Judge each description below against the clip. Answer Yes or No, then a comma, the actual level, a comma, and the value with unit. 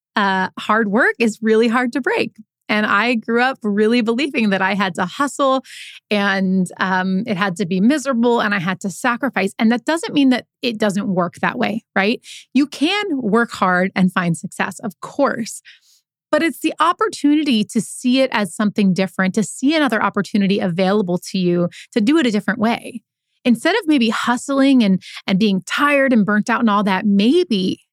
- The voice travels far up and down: No, average, 4.8 semitones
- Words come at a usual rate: Yes, average, 190 wpm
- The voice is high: Yes, high, 220 Hz